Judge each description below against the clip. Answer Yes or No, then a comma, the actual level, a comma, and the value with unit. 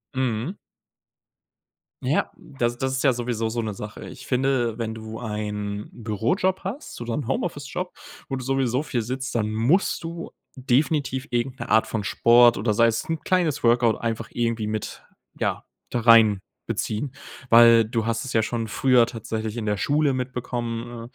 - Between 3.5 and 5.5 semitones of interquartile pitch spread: No, average, 2.9 semitones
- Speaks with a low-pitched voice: Yes, low, 120 Hz